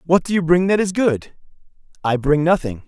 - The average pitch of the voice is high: No, medium, 165 Hz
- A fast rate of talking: Yes, fast, 210 wpm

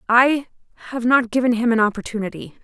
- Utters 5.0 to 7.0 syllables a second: Yes, 6.0 syllables/s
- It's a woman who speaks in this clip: Yes, female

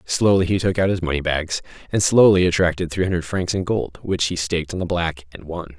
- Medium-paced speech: No, fast, 240 wpm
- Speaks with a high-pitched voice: No, very low, 90 Hz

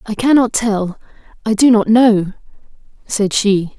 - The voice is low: No, high, 215 Hz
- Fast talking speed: No, average, 145 wpm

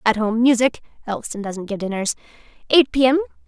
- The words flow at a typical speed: Yes, average, 175 wpm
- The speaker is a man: No, female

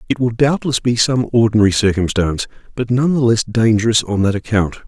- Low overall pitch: Yes, low, 115 Hz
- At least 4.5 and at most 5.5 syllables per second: No, 5.8 syllables/s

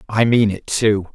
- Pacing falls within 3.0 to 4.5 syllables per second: Yes, 4.4 syllables/s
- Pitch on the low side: Yes, low, 105 Hz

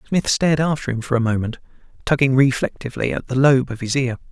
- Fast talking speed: Yes, fast, 210 wpm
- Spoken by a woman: No, male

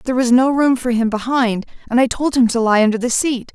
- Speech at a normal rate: No, fast, 270 wpm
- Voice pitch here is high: Yes, high, 245 Hz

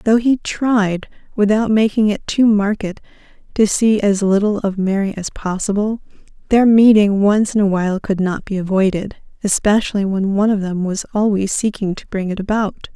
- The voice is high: Yes, high, 205 Hz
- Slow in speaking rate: No, average, 175 wpm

